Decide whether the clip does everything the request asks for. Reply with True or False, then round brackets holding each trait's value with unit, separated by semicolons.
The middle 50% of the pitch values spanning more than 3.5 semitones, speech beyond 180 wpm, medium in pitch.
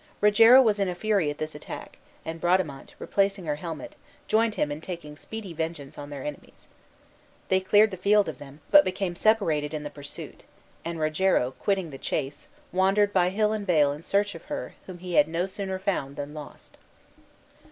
True (5.1 semitones; 190 wpm; 175 Hz)